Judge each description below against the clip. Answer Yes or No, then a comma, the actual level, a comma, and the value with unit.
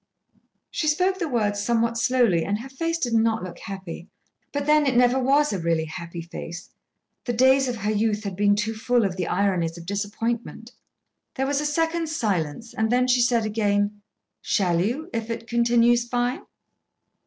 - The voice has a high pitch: Yes, high, 230 Hz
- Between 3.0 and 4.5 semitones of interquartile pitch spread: Yes, average, 4.0 semitones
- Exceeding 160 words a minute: Yes, average, 180 wpm